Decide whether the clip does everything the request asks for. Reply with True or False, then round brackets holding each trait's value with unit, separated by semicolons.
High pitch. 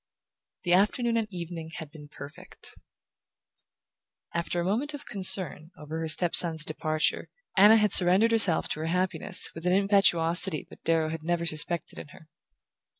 False (175 Hz)